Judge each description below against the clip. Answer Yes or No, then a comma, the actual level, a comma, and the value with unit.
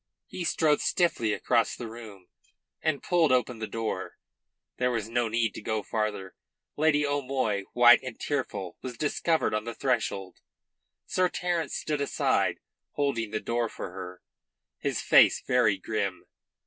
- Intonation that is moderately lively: Yes, average, 4.9 semitones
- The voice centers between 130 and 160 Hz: No, low, 120 Hz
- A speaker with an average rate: Yes, average, 150 wpm